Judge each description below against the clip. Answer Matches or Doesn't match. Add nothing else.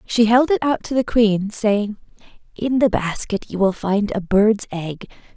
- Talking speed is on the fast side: Doesn't match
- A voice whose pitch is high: Matches